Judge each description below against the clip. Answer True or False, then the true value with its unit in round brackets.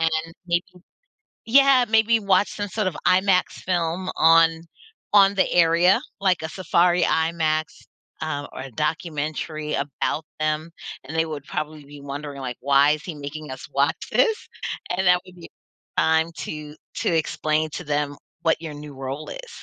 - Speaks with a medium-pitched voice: True (160 Hz)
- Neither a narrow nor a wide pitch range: True (3.4 semitones)